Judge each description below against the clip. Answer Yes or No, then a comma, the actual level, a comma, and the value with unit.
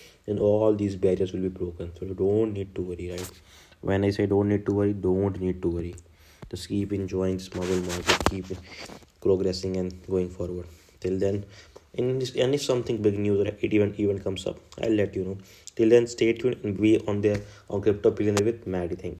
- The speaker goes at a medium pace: No, fast, 215 wpm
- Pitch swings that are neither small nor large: No, narrow, 2.1 semitones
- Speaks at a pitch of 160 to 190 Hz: No, very low, 95 Hz